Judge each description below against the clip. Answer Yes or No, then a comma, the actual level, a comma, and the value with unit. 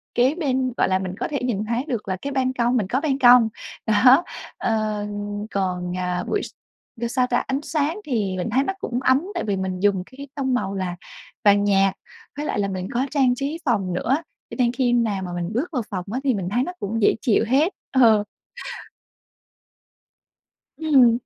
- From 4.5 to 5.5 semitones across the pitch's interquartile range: Yes, average, 5.1 semitones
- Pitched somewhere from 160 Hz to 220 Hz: No, high, 235 Hz